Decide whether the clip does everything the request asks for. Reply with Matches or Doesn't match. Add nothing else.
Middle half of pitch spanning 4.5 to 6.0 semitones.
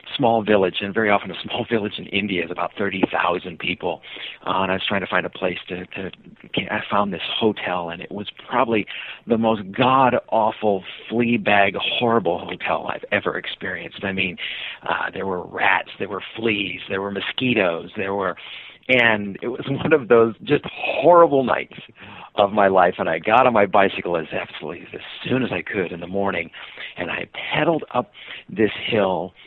Doesn't match